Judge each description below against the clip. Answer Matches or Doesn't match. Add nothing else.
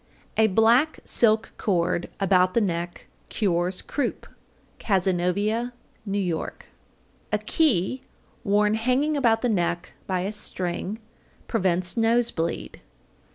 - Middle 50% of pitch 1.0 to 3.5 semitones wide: Doesn't match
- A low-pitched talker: Doesn't match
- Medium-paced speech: Doesn't match